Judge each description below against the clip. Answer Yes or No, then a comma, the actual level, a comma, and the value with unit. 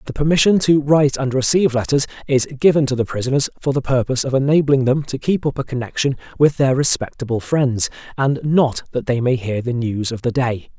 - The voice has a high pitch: No, low, 135 Hz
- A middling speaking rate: No, fast, 210 wpm